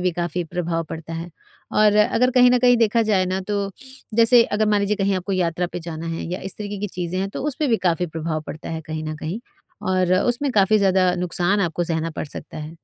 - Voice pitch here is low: No, medium, 185 Hz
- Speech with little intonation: No, average, 4.0 semitones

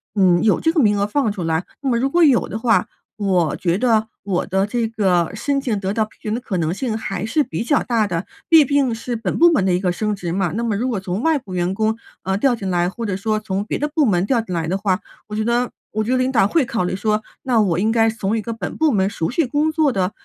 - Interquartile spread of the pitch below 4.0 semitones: No, average, 4.3 semitones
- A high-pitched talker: Yes, high, 215 Hz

